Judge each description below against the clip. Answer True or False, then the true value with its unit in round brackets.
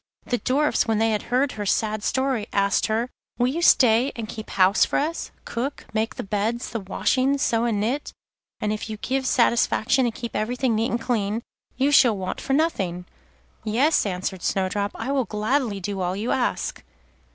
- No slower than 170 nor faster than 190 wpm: True (185 wpm)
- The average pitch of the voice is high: True (225 Hz)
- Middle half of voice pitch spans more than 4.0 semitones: False (3.7 semitones)